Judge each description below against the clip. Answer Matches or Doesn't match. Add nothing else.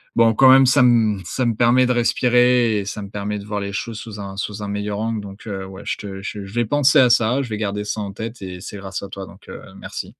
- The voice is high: Doesn't match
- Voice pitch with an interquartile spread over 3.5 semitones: Doesn't match